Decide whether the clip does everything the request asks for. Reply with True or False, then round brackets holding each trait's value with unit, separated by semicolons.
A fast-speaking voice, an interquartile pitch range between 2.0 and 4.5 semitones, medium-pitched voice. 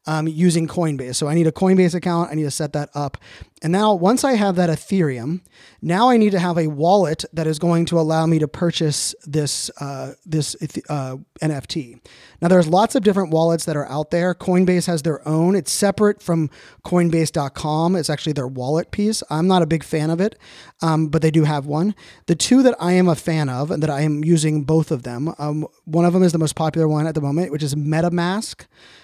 True (225 wpm; 2.7 semitones; 160 Hz)